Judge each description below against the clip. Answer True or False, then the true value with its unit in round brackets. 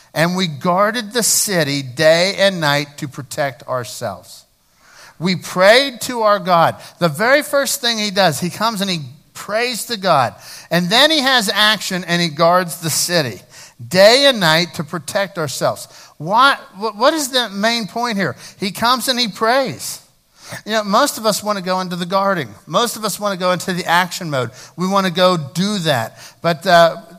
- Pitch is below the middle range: False (185 Hz)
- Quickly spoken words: False (190 wpm)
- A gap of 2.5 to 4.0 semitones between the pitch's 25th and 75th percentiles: False (5.1 semitones)